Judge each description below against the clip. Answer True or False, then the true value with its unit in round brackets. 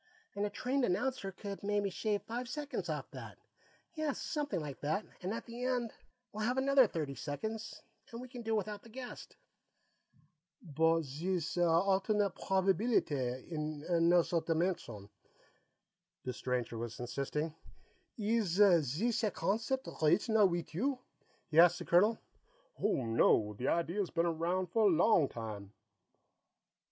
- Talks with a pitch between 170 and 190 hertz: True (185 Hz)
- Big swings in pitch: True (6.0 semitones)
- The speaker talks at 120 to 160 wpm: True (140 wpm)